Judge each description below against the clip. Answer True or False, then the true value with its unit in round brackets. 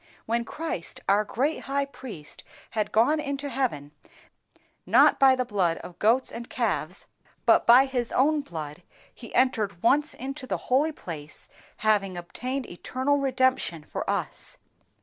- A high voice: True (250 Hz)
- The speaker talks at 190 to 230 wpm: False (145 wpm)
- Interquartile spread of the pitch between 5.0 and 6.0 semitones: True (5.5 semitones)